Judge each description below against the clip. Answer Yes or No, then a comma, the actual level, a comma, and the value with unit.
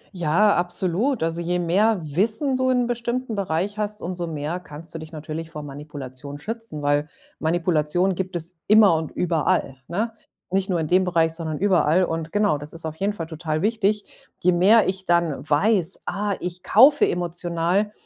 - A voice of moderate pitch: Yes, medium, 175 Hz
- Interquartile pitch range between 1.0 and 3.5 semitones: No, average, 4.4 semitones